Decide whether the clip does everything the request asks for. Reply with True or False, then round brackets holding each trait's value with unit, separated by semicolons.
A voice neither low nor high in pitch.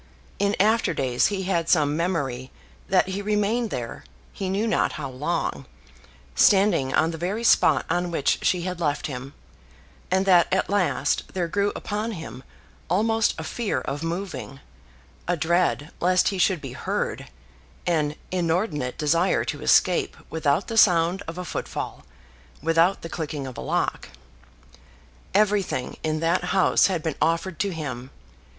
True (170 Hz)